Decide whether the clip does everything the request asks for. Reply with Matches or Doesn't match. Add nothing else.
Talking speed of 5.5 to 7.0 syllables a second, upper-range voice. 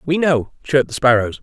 Doesn't match